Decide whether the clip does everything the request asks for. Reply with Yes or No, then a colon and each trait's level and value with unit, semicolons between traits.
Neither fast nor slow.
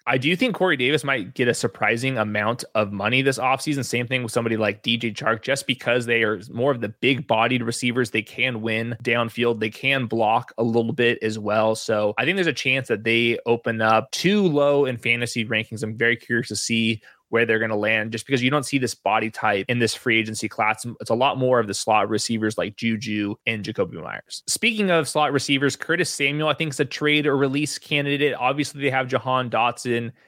No: fast, 225 wpm